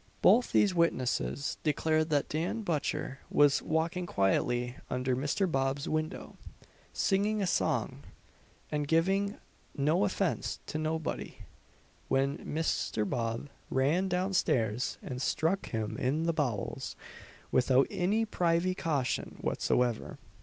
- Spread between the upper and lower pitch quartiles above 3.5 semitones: Yes, average, 5.3 semitones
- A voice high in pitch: No, medium, 155 Hz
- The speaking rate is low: Yes, slow, 115 wpm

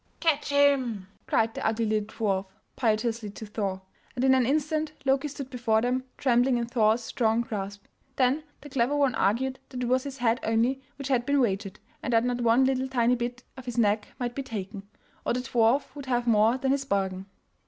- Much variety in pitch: No, average, 3.2 semitones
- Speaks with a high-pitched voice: Yes, high, 245 Hz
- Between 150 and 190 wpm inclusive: No, fast, 205 wpm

